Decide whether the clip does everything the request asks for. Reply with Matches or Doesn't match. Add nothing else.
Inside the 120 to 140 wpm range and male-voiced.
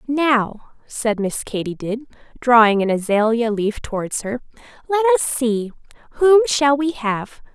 Doesn't match